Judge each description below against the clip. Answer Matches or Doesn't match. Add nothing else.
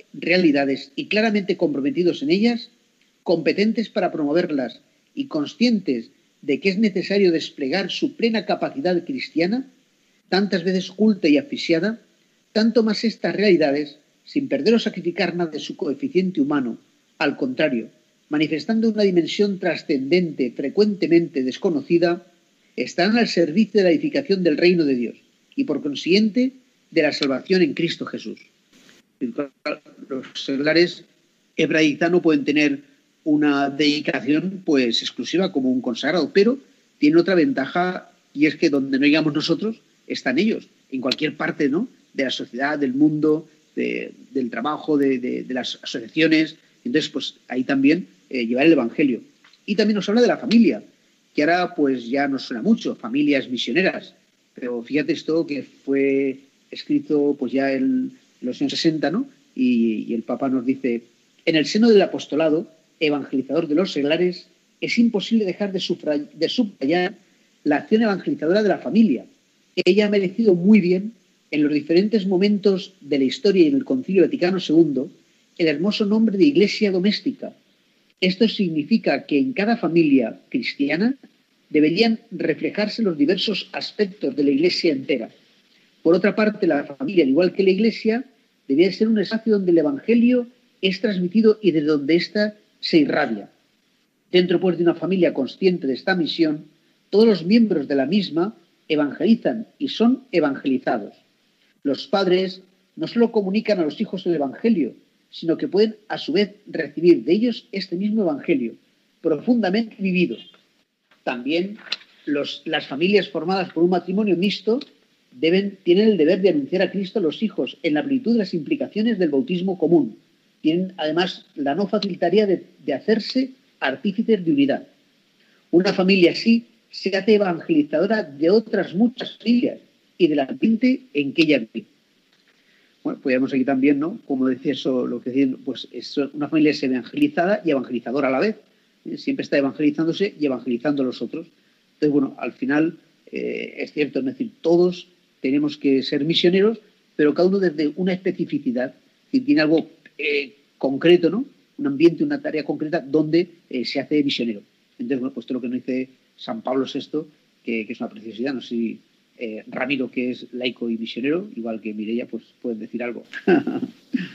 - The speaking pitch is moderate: Matches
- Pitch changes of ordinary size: Doesn't match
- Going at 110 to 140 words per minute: Doesn't match